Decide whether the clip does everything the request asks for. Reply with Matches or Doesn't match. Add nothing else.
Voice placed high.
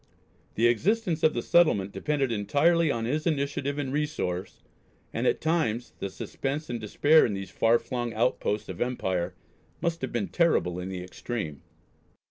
Doesn't match